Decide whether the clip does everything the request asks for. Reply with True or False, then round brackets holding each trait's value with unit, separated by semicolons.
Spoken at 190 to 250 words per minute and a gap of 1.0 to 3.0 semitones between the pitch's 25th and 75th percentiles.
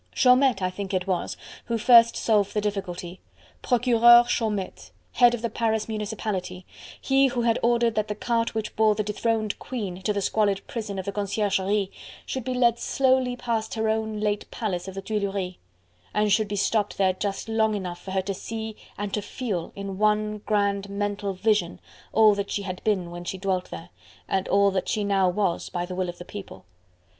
True (195 wpm; 2.6 semitones)